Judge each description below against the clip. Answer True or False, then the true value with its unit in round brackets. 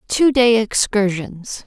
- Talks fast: False (110 wpm)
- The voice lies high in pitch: True (215 Hz)